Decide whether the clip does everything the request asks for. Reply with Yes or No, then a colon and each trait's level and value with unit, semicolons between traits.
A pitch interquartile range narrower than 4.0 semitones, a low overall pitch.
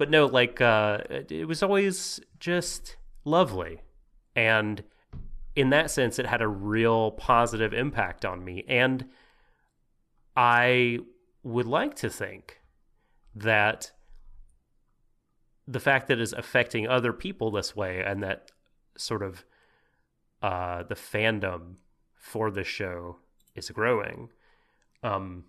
No: average, 5.2 semitones; low, 110 Hz